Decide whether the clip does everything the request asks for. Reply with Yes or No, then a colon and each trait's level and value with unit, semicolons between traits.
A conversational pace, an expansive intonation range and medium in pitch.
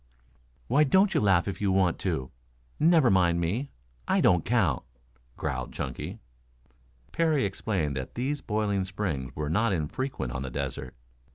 No: average, 150 wpm; wide, 7.8 semitones; very low, 95 Hz